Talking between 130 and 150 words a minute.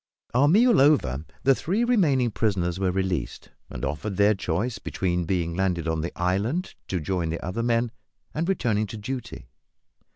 No: average, 165 wpm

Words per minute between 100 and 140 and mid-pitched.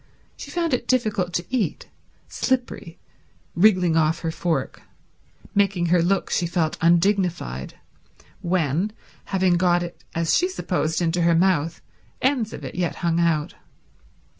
Yes: slow, 135 wpm; medium, 175 Hz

